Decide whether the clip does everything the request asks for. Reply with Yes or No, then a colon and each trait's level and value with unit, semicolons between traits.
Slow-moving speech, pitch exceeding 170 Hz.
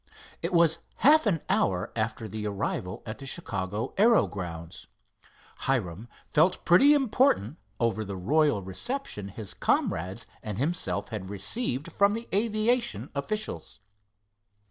No: slow, 125 wpm; low, 125 Hz